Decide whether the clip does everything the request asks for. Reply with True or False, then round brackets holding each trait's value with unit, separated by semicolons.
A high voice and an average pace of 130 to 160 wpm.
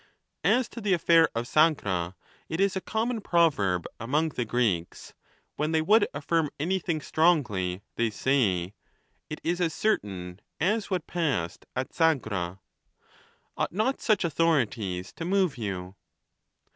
False (150 Hz; 140 wpm)